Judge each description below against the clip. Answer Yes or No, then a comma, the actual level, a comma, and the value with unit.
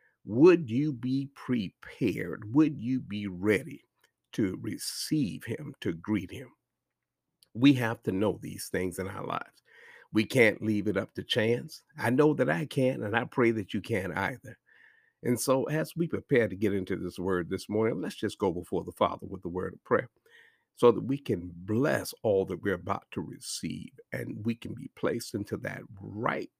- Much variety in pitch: No, average, 4.9 semitones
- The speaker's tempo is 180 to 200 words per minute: Yes, average, 190 wpm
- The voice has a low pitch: Yes, low, 110 Hz